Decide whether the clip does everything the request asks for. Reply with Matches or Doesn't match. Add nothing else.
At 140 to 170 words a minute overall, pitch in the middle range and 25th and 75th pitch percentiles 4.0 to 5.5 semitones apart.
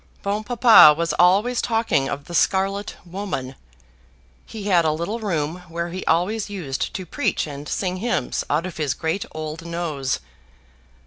Matches